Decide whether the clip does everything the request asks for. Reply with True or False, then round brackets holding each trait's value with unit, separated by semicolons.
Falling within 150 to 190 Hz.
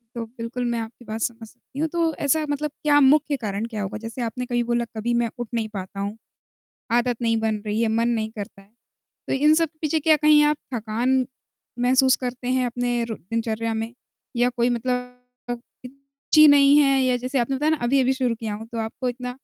False (240 Hz)